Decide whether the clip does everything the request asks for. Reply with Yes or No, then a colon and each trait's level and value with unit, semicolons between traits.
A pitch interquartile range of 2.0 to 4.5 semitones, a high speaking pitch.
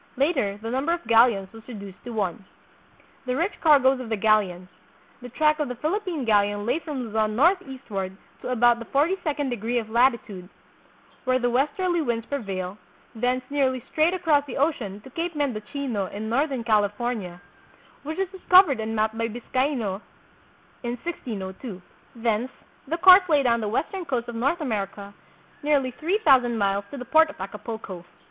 No: average, 5.2 semitones; high, 245 Hz